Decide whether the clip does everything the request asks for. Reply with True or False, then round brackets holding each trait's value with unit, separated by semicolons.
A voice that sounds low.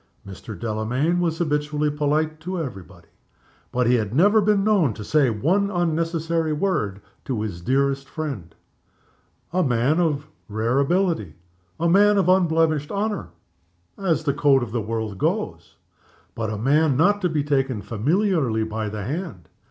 False (150 Hz)